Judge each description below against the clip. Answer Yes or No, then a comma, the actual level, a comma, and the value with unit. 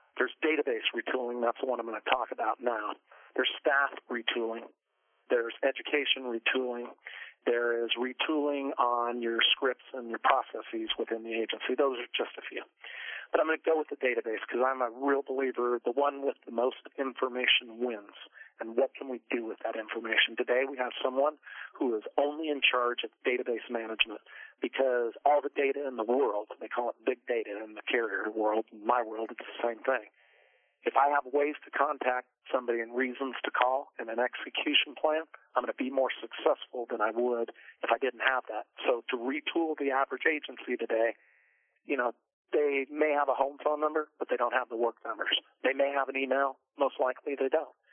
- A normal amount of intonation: Yes, average, 3.2 semitones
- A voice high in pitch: No, low, 130 Hz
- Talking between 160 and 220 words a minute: Yes, average, 200 wpm